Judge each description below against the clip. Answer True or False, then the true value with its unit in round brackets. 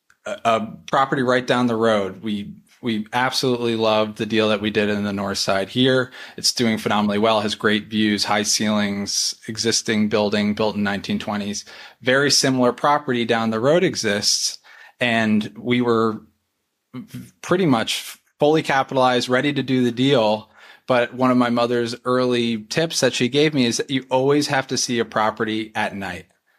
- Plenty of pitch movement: False (3.1 semitones)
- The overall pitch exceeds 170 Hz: False (115 Hz)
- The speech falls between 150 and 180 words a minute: True (170 wpm)